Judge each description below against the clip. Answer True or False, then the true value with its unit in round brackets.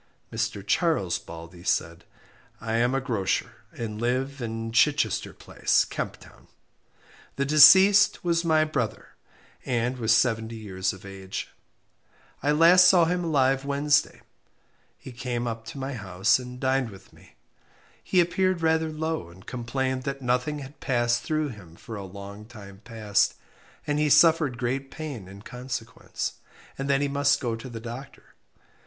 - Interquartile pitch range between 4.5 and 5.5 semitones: True (4.8 semitones)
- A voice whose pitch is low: True (125 Hz)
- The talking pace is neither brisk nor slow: True (155 wpm)